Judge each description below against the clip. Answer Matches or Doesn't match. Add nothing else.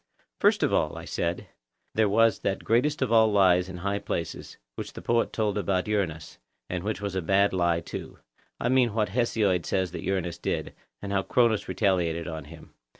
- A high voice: Doesn't match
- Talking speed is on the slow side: Doesn't match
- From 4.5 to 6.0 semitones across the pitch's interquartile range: Doesn't match